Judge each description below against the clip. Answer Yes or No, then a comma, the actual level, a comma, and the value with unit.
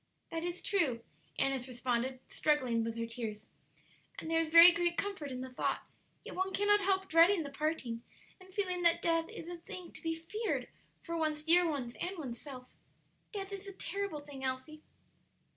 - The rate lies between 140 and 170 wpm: No, average, 185 wpm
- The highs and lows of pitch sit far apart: Yes, wide, 5.7 semitones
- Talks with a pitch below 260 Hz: No, very high, 325 Hz